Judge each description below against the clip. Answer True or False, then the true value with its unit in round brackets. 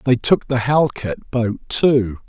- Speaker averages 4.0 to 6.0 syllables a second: False (3.5 syllables/s)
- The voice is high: False (125 Hz)